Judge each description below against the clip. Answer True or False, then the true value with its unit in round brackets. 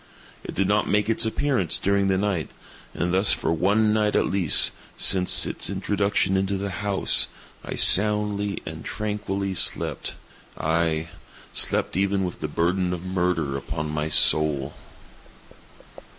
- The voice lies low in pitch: True (95 Hz)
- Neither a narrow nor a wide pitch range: True (3.4 semitones)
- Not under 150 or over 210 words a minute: False (140 wpm)